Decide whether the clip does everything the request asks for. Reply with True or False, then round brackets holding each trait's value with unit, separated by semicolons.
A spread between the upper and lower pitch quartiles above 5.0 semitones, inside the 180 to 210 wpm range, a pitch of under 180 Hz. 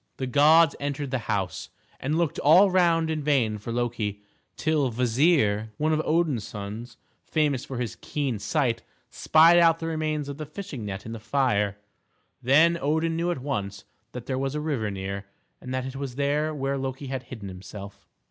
True (5.5 semitones; 185 wpm; 135 Hz)